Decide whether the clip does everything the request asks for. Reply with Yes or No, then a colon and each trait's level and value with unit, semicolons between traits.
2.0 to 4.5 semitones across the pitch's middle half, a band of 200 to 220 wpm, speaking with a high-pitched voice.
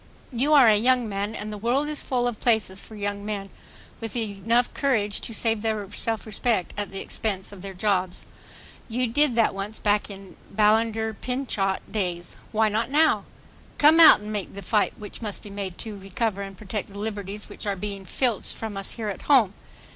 Yes: narrow, 2.5 semitones; fast, 205 wpm; high, 210 Hz